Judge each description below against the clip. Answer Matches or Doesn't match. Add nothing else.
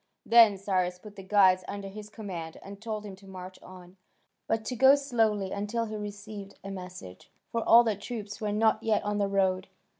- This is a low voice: Doesn't match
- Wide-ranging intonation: Doesn't match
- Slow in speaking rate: Doesn't match